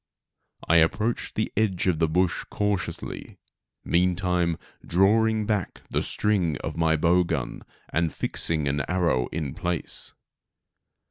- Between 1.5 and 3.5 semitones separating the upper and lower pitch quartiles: Yes, average, 3.2 semitones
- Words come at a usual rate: No, slow, 125 wpm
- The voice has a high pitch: No, very low, 90 Hz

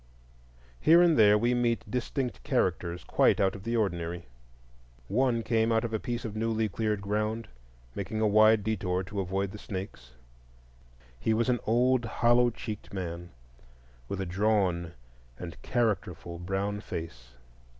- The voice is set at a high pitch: No, low, 105 Hz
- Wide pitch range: No, average, 3.7 semitones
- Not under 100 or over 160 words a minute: Yes, average, 150 wpm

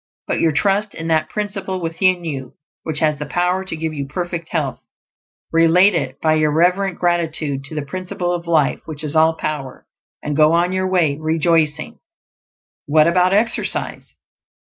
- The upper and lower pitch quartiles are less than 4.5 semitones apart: Yes, average, 2.8 semitones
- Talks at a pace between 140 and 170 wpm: Yes, average, 165 wpm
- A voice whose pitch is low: No, medium, 165 Hz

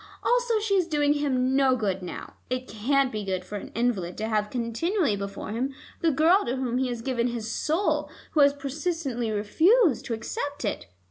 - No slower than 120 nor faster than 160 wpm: No, average, 195 wpm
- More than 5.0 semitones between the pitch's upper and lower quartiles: Yes, wide, 5.5 semitones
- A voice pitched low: No, very high, 255 Hz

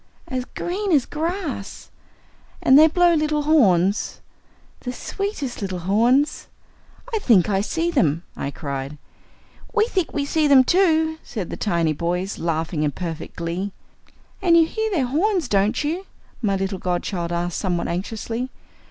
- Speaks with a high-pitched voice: Yes, high, 240 Hz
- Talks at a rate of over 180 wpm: No, average, 150 wpm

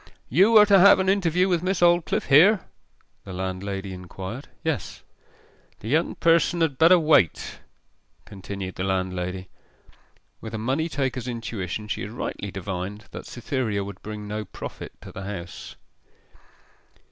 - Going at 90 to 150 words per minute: Yes, average, 145 wpm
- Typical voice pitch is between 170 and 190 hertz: No, low, 110 Hz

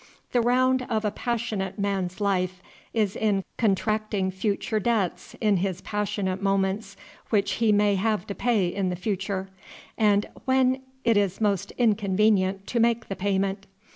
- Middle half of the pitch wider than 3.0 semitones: No, narrow, 2.4 semitones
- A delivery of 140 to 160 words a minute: Yes, average, 145 wpm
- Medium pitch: No, high, 205 Hz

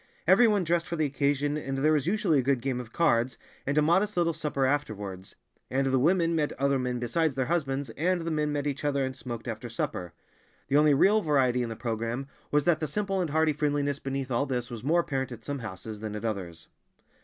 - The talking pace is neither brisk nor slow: No, fast, 225 wpm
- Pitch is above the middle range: No, medium, 140 Hz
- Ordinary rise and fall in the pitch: Yes, average, 4.1 semitones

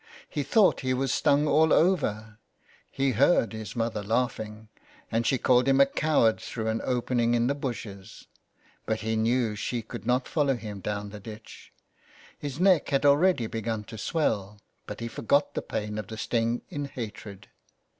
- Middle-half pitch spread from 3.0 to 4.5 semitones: Yes, average, 3.9 semitones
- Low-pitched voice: Yes, low, 115 Hz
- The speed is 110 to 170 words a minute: No, average, 180 wpm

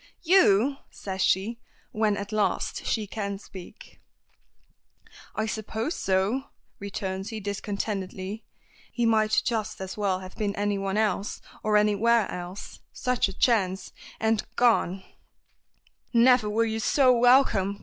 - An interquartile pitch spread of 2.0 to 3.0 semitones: Yes, narrow, 2.6 semitones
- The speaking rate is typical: No, slow, 125 wpm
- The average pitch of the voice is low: No, high, 210 Hz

